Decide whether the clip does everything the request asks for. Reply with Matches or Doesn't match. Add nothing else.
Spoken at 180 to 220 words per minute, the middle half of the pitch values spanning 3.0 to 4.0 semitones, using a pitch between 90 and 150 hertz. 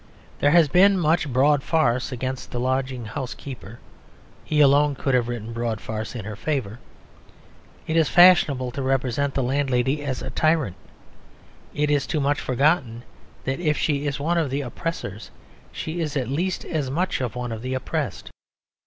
Doesn't match